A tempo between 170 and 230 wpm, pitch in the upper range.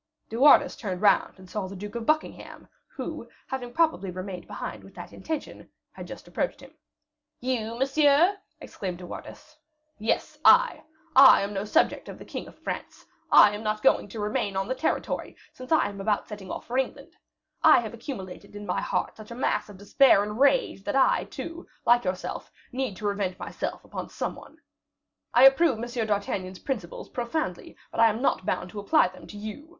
Yes: average, 195 wpm; high, 220 Hz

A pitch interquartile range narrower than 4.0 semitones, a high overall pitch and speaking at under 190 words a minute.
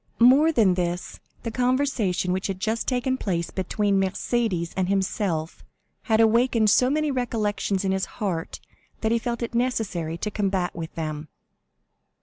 No: average, 4.6 semitones; high, 205 Hz; average, 150 wpm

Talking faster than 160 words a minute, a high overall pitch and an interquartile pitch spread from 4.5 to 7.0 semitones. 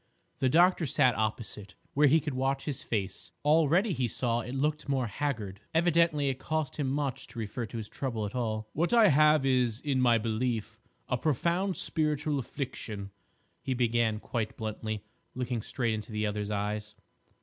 No: average, 170 wpm; low, 125 Hz; average, 5.3 semitones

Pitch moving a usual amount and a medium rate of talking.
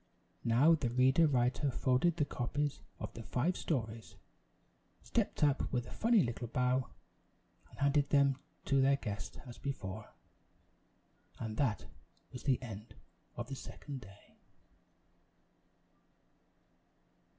No: average, 3.3 semitones; slow, 120 wpm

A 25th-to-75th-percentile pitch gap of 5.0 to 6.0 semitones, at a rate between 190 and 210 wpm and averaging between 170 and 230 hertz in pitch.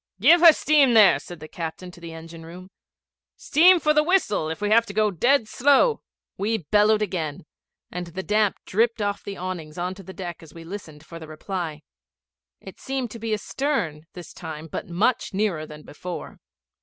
Yes: wide, 5.4 semitones; average, 195 wpm; high, 190 Hz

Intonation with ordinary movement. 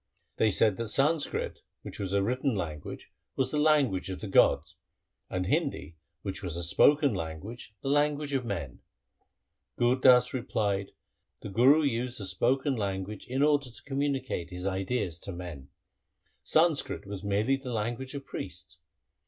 No: wide, 6.1 semitones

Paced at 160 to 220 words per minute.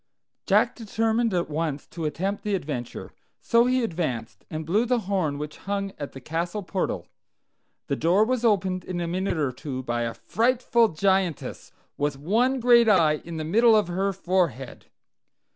Yes: average, 170 wpm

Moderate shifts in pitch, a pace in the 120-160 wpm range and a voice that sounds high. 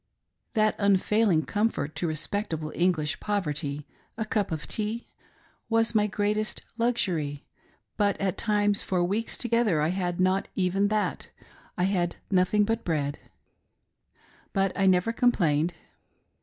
Yes: average, 3.8 semitones; average, 140 wpm; high, 195 Hz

